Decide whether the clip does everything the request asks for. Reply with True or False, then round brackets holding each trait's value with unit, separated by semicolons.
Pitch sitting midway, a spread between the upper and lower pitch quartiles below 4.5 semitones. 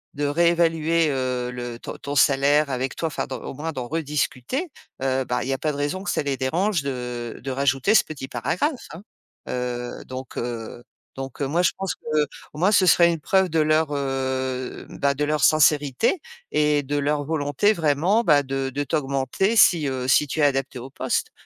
True (145 Hz; 3.5 semitones)